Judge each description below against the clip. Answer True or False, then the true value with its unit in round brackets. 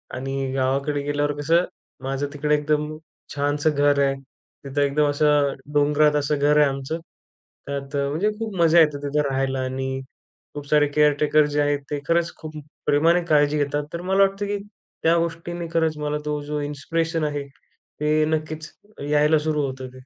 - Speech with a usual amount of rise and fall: False (1.7 semitones)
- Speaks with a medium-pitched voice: True (150 Hz)